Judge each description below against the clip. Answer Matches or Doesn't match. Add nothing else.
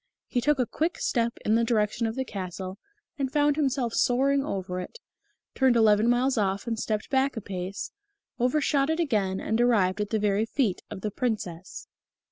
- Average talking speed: Matches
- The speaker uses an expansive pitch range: Doesn't match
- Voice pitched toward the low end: Doesn't match